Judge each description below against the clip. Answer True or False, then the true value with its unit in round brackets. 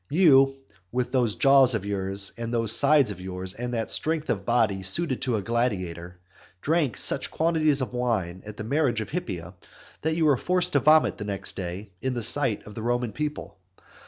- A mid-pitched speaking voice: False (120 Hz)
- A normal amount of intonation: False (5.9 semitones)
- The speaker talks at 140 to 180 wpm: False (195 wpm)